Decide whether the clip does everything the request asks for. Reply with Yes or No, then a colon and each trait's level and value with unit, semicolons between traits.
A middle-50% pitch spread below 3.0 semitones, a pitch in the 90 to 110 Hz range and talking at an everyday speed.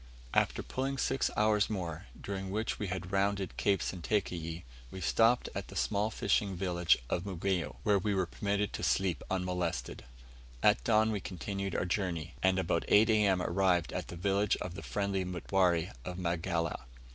Yes: narrow, 2.6 semitones; very low, 95 Hz; average, 170 wpm